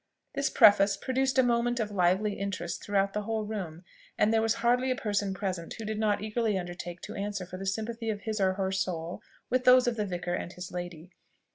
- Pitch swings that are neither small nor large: Yes, average, 3.3 semitones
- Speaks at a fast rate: Yes, fast, 220 wpm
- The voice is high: Yes, high, 205 Hz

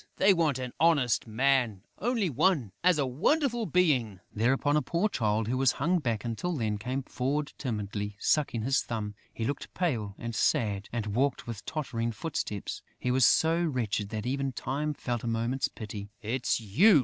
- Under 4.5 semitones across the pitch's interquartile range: No, average, 5.3 semitones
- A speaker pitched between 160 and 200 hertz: No, low, 125 Hz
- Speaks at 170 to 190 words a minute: Yes, average, 175 wpm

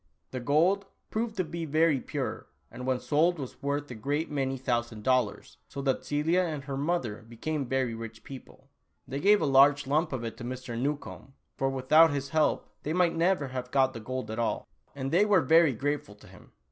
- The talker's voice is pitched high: No, medium, 140 Hz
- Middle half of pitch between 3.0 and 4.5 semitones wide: Yes, average, 3.7 semitones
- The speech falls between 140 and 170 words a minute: No, fast, 205 wpm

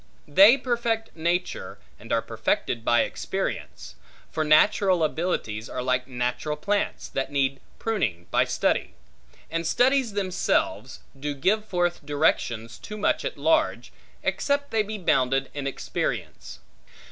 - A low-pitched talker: No, medium, 165 Hz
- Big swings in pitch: Yes, wide, 8.0 semitones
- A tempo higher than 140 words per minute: No, slow, 135 wpm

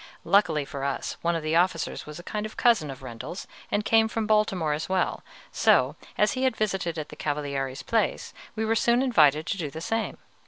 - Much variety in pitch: Yes, wide, 6.3 semitones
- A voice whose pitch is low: No, medium, 175 Hz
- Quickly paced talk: Yes, fast, 210 wpm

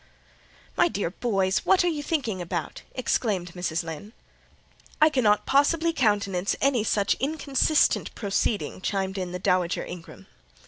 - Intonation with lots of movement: Yes, wide, 7.2 semitones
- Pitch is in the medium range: No, high, 205 Hz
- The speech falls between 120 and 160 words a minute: Yes, slow, 135 wpm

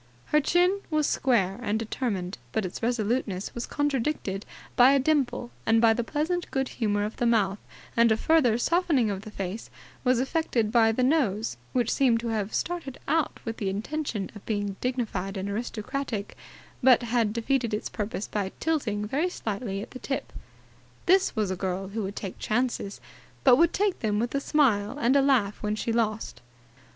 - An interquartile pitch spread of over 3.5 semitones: Yes, average, 4.5 semitones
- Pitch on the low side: No, high, 230 Hz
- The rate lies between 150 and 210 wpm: Yes, average, 180 wpm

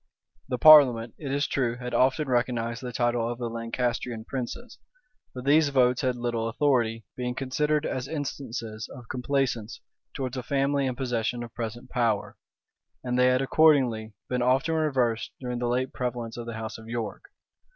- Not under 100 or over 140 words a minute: No, average, 170 wpm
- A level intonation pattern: Yes, narrow, 2.3 semitones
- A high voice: No, low, 125 Hz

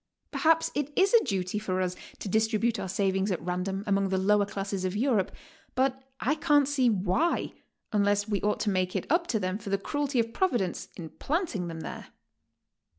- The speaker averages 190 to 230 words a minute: Yes, average, 195 wpm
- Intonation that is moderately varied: No, wide, 5.7 semitones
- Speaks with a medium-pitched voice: No, high, 205 Hz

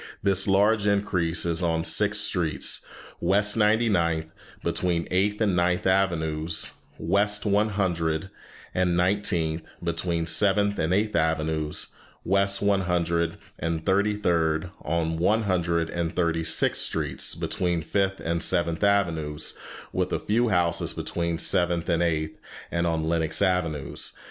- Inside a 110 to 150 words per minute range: Yes, average, 140 wpm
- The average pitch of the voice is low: Yes, very low, 85 Hz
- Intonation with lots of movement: No, average, 3.2 semitones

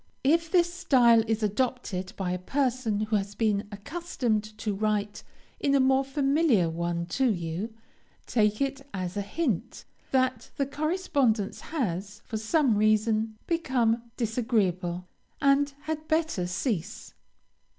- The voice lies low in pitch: No, high, 225 Hz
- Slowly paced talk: Yes, slow, 130 wpm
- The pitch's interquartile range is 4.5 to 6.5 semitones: Yes, average, 5.3 semitones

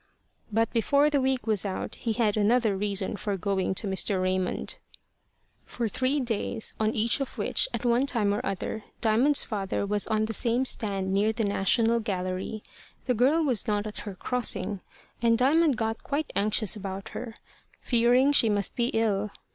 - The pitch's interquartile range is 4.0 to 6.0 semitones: No, average, 3.3 semitones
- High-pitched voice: Yes, high, 220 Hz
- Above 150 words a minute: Yes, average, 175 wpm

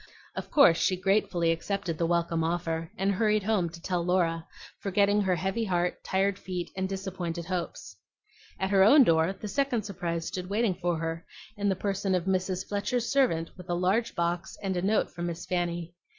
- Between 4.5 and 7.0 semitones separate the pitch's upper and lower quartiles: No, average, 2.7 semitones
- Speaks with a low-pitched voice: No, medium, 185 Hz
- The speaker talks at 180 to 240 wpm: Yes, average, 190 wpm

